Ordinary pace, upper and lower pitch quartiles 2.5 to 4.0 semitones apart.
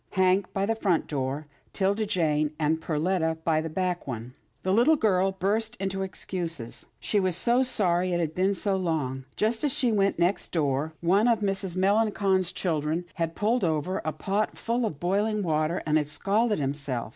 No: average, 180 wpm; average, 4.4 semitones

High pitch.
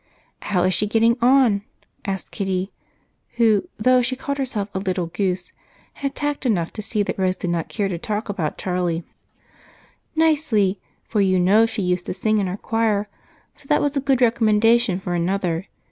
Yes: high, 205 Hz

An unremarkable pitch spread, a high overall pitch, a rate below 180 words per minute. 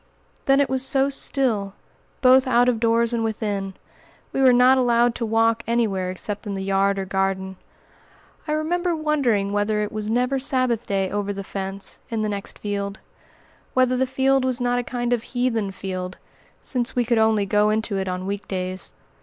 No: average, 4.2 semitones; high, 225 Hz; average, 185 wpm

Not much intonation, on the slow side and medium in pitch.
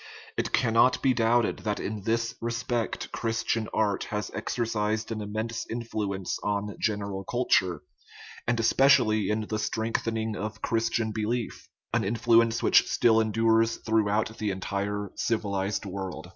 No: narrow, 1.8 semitones; slow, 130 wpm; low, 110 Hz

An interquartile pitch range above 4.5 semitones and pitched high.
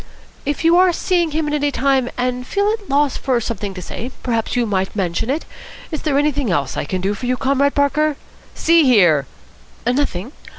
Yes: wide, 5.4 semitones; very high, 265 Hz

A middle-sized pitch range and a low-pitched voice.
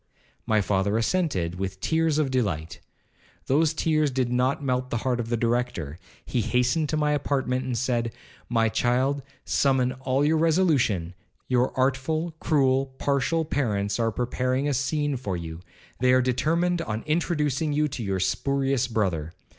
Yes: average, 4.3 semitones; low, 130 Hz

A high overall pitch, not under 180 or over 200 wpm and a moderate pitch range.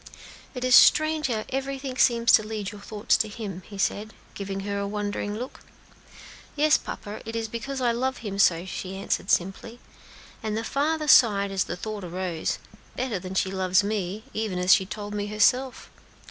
Yes: high, 210 Hz; average, 185 wpm; average, 3.7 semitones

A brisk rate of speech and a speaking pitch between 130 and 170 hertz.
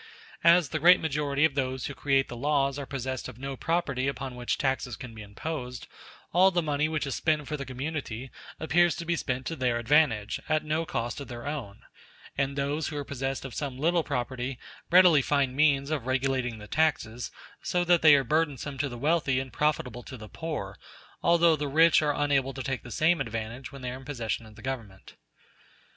Yes: fast, 210 wpm; medium, 140 Hz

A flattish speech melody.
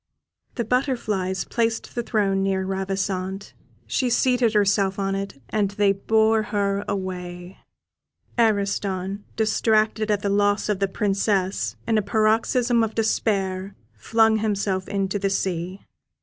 Yes: narrow, 2.2 semitones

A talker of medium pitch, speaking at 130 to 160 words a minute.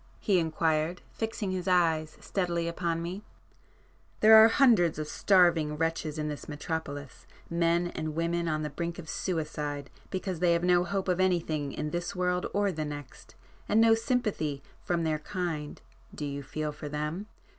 Yes: medium, 170 Hz; average, 155 wpm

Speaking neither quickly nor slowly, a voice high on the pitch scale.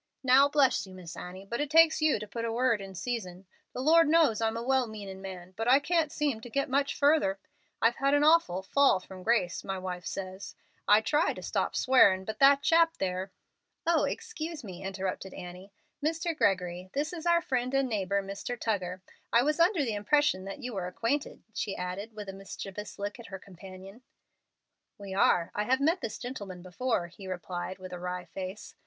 No: fast, 210 wpm; high, 215 Hz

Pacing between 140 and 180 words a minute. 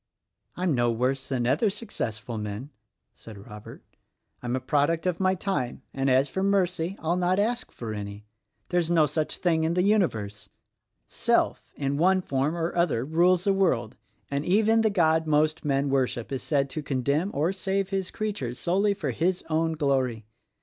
Yes: average, 175 wpm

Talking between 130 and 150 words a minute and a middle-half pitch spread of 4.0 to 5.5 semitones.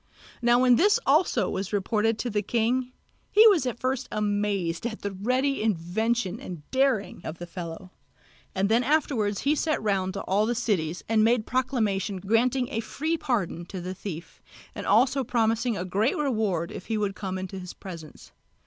No: average, 180 wpm; average, 4.6 semitones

